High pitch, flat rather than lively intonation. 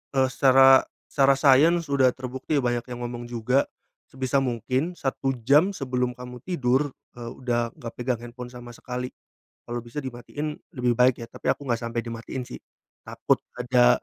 No: low, 125 Hz; narrow, 1.9 semitones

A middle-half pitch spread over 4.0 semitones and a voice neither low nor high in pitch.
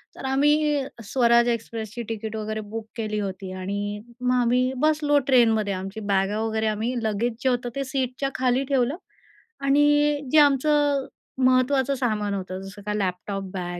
No: average, 4.6 semitones; high, 235 Hz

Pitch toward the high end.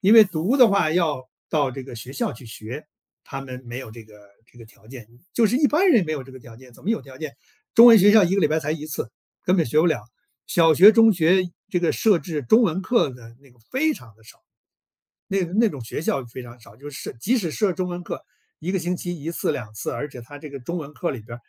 No: medium, 155 Hz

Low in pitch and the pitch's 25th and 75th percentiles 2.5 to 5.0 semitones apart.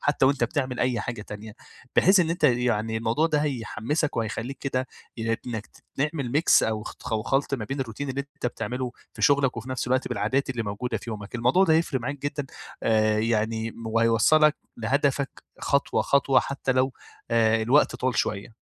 Yes: low, 125 Hz; average, 3.7 semitones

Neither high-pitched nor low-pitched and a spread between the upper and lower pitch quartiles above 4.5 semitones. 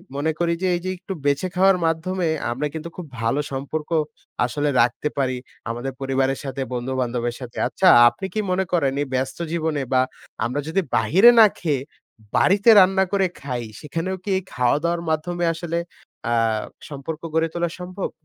Yes: medium, 155 Hz; average, 5.1 semitones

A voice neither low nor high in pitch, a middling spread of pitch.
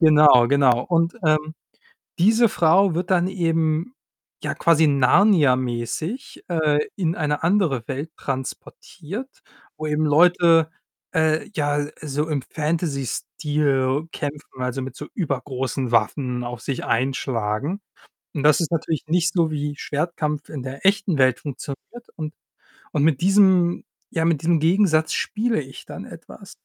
Yes: medium, 155 Hz; average, 3.7 semitones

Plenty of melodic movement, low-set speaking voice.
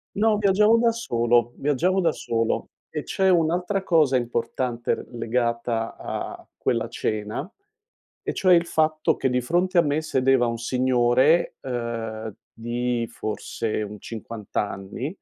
Yes: wide, 6.4 semitones; low, 125 Hz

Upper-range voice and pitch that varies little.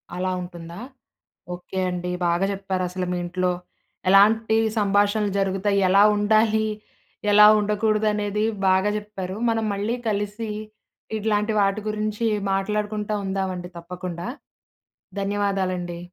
Yes: high, 200 Hz; narrow, 2.3 semitones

